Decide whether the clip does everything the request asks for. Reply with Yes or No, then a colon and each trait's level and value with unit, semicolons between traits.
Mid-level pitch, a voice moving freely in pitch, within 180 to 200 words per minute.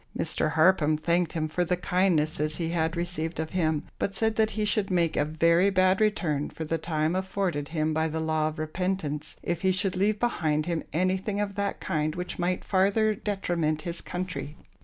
No: medium, 170 Hz; average, 3.3 semitones; average, 195 wpm